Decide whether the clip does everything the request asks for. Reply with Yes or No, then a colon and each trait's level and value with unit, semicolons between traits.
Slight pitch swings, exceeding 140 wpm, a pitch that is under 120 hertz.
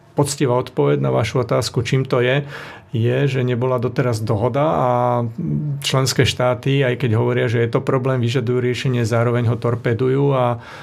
No: narrow, 2.1 semitones; average, 160 wpm; low, 125 Hz